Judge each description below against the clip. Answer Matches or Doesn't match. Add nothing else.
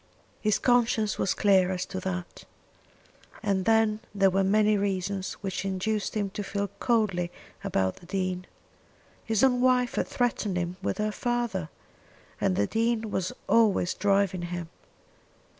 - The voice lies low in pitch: Doesn't match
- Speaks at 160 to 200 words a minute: Doesn't match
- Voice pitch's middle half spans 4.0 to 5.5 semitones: Doesn't match